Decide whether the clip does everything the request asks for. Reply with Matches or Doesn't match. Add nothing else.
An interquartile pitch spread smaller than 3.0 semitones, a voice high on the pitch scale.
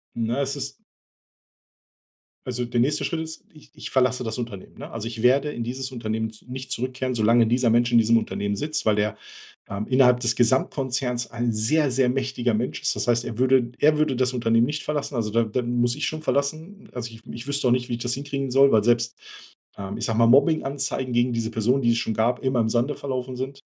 Doesn't match